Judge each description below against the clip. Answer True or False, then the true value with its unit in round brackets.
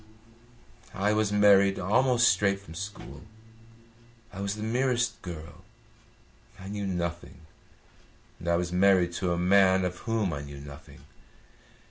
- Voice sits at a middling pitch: False (95 Hz)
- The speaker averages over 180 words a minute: False (135 wpm)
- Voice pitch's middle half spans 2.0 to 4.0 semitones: True (2.9 semitones)